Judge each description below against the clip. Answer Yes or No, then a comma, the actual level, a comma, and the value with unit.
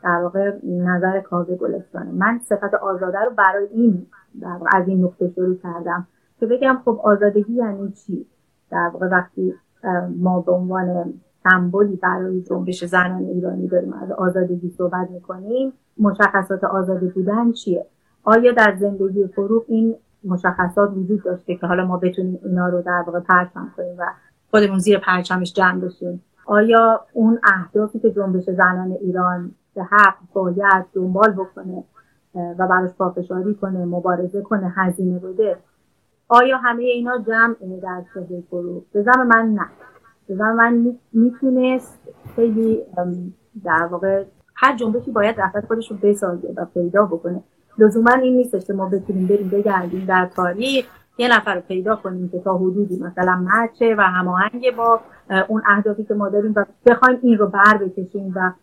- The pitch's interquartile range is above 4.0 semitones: No, average, 3.2 semitones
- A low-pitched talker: No, high, 195 Hz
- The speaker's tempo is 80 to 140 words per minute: No, average, 150 wpm